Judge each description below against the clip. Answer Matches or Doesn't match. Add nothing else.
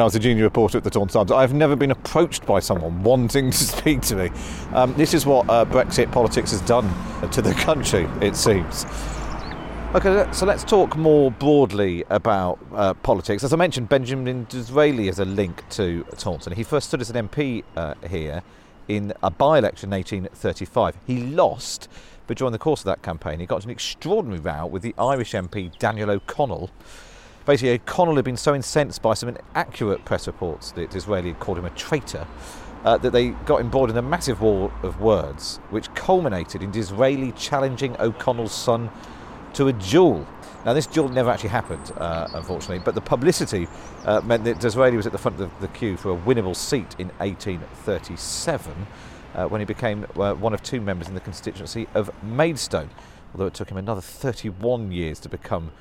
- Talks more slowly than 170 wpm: Doesn't match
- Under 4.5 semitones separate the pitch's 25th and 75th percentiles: Doesn't match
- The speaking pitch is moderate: Doesn't match